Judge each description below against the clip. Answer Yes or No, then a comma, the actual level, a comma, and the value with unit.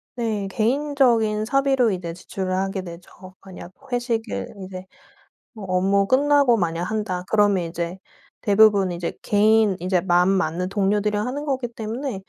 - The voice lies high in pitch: Yes, high, 205 Hz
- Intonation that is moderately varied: Yes, average, 3.8 semitones